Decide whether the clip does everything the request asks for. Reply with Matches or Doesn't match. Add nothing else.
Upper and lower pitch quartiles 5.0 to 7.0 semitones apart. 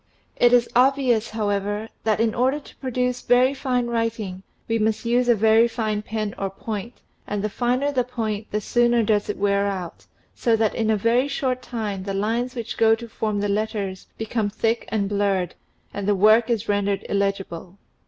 Doesn't match